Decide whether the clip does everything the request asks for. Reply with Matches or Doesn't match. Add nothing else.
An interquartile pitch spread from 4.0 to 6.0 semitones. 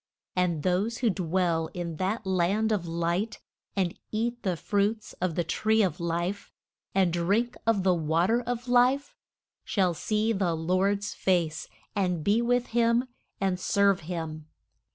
Matches